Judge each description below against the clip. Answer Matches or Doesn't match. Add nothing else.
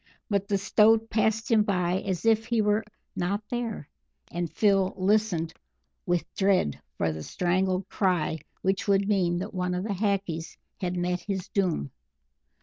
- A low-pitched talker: Doesn't match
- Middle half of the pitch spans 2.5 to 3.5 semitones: Matches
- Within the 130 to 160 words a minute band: Matches